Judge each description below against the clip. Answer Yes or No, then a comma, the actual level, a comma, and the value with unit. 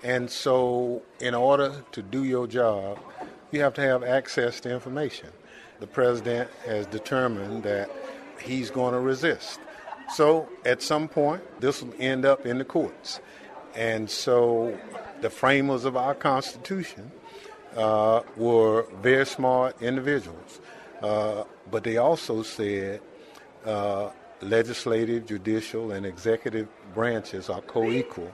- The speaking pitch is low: Yes, low, 120 Hz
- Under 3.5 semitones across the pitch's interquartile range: Yes, average, 3.0 semitones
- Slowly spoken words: Yes, slow, 130 wpm